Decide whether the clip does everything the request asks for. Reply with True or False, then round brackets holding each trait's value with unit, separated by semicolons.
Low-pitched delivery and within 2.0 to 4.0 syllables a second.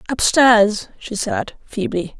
False (225 Hz; 3.3 syllables/s)